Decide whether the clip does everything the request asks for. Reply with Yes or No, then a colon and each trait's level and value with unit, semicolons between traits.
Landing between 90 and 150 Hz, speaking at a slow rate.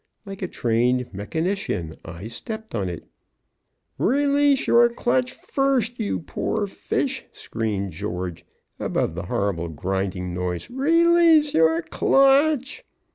No: medium, 170 Hz; slow, 115 wpm